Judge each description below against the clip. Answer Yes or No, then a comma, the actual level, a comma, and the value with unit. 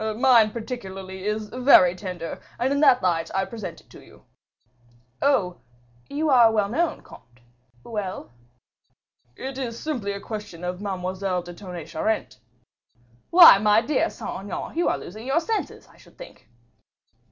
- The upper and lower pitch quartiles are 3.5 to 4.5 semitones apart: No, wide, 5.5 semitones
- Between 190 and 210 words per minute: No, average, 150 wpm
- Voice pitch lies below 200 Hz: No, high, 210 Hz